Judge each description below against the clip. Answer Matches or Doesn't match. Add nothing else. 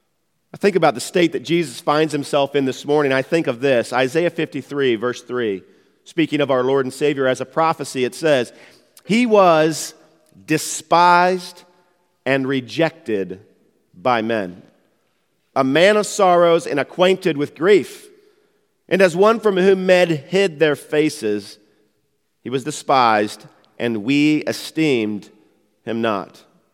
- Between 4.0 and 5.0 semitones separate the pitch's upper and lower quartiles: Doesn't match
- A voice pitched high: Doesn't match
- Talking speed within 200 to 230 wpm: Doesn't match